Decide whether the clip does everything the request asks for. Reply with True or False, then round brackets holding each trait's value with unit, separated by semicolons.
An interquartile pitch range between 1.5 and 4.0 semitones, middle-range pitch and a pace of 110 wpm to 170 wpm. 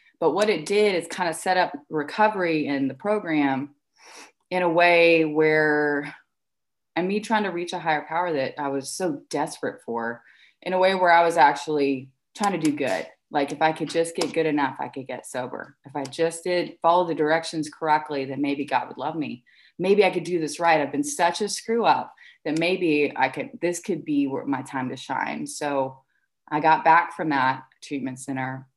False (3.5 semitones; 155 Hz; 205 wpm)